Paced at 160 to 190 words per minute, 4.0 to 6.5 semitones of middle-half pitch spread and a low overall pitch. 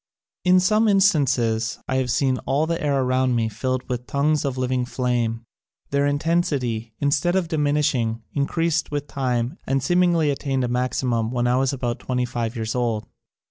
No: average, 175 wpm; average, 3.3 semitones; low, 130 Hz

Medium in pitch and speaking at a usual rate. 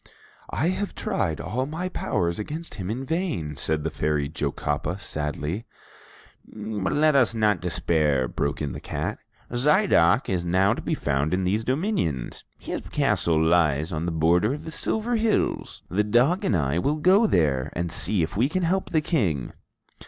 No: very low, 95 Hz; average, 175 wpm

